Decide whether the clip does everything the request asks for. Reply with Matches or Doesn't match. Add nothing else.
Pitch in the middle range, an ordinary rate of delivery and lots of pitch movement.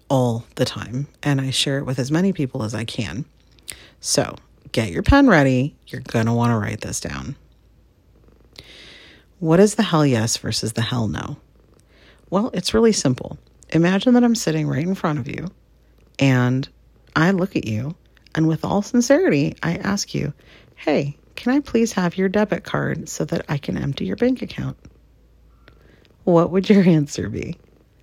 Matches